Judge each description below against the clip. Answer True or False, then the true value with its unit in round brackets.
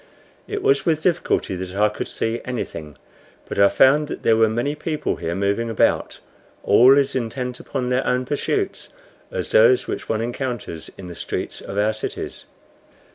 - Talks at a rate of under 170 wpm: False (175 wpm)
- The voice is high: False (125 Hz)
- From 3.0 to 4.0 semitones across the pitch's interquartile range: False (5.6 semitones)